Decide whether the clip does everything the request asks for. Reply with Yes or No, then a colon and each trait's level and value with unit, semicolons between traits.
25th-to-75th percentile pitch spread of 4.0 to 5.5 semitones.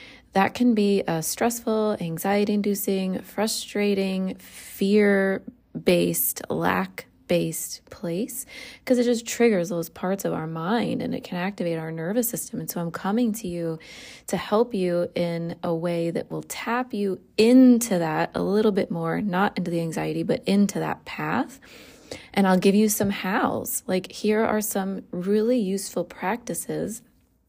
Yes: average, 4.7 semitones